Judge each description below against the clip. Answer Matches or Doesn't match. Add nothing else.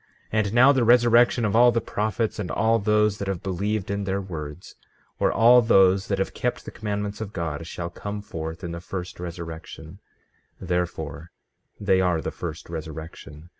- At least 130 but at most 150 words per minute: Doesn't match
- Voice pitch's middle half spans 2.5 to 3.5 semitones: Doesn't match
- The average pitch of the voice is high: Doesn't match